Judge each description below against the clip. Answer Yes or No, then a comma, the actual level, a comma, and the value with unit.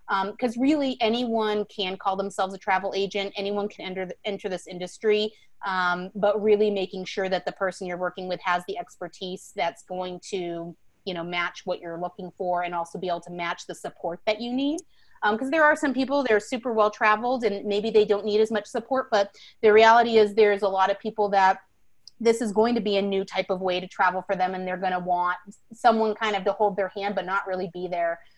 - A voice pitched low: No, high, 195 Hz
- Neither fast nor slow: No, fast, 235 wpm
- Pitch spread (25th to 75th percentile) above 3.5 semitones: No, average, 2.7 semitones